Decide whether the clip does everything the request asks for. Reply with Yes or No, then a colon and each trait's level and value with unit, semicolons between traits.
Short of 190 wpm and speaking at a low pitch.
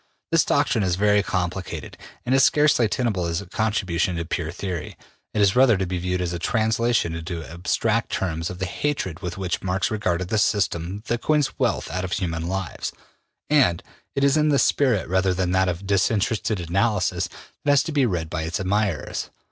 No: average, 195 wpm; very low, 95 Hz